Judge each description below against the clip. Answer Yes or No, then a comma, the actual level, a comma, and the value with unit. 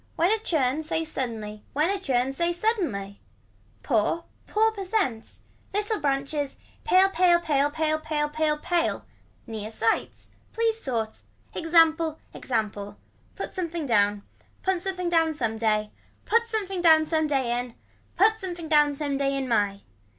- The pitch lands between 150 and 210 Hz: No, very high, 310 Hz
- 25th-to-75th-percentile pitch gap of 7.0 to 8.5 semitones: No, wide, 6.2 semitones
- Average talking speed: Yes, average, 145 wpm